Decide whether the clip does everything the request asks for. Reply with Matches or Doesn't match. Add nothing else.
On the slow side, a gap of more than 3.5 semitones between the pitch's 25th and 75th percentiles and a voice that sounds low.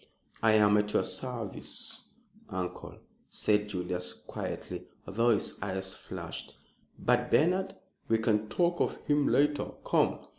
Matches